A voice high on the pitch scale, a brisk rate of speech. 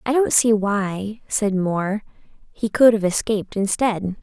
No: high, 210 Hz; average, 155 wpm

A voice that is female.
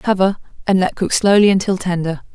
Yes: female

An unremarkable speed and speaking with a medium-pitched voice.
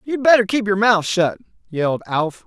No: average, 195 wpm; high, 195 Hz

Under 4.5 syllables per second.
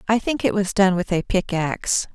No: 5.2 syllables/s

